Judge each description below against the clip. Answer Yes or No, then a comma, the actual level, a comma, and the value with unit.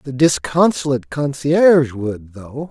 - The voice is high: No, medium, 140 Hz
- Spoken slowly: Yes, slow, 110 wpm